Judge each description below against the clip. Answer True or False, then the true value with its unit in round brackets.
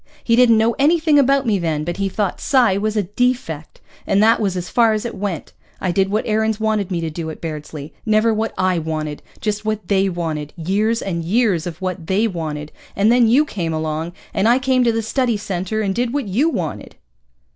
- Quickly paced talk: True (220 wpm)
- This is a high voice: True (205 Hz)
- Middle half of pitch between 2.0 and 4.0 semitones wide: False (5.0 semitones)